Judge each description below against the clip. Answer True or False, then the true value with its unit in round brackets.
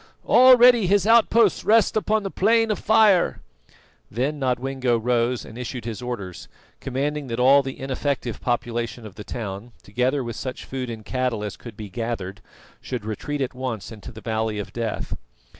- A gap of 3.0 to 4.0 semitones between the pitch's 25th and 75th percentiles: False (4.5 semitones)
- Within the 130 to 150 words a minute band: False (170 wpm)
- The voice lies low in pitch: True (125 Hz)